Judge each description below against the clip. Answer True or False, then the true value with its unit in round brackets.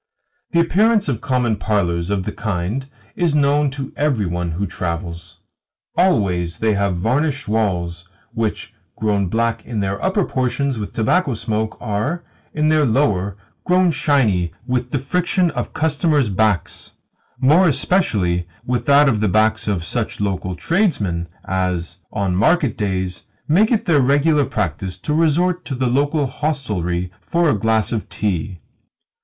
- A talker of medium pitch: False (115 Hz)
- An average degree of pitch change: False (7.6 semitones)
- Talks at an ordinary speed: True (150 wpm)